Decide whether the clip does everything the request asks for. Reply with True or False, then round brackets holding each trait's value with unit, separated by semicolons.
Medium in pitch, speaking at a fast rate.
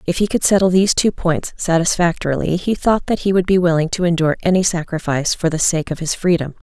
True (175 Hz; 225 wpm)